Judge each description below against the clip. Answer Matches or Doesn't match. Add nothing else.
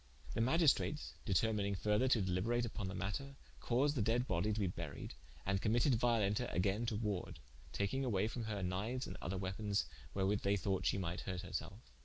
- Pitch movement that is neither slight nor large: Matches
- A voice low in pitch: Matches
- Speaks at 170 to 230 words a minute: Matches